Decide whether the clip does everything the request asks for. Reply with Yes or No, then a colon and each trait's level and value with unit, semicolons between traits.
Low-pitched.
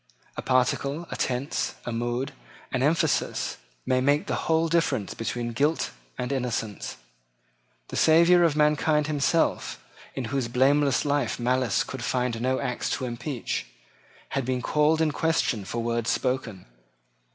Yes: low, 130 Hz